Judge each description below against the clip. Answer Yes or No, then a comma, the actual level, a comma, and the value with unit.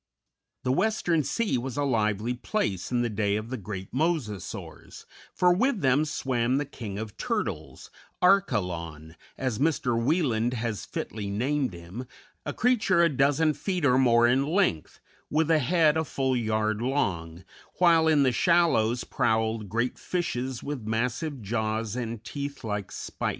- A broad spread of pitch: Yes, wide, 5.8 semitones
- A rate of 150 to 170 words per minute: Yes, average, 155 wpm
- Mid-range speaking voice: No, low, 125 Hz